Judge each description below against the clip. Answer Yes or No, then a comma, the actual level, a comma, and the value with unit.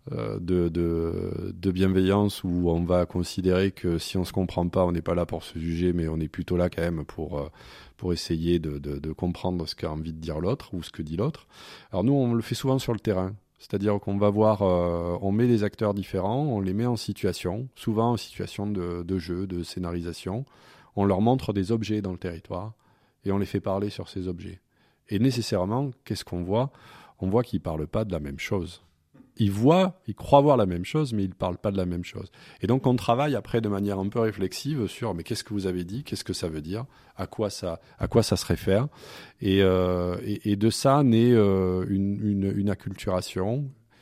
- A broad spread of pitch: No, average, 4.2 semitones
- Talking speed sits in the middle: No, fast, 230 wpm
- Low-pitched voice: Yes, very low, 95 Hz